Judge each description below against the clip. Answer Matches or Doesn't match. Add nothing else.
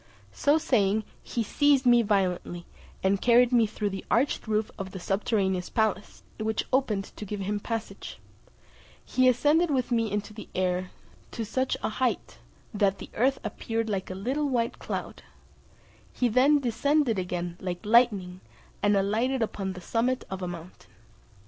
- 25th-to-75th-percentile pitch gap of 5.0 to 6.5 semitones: Doesn't match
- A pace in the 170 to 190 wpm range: Doesn't match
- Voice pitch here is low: Doesn't match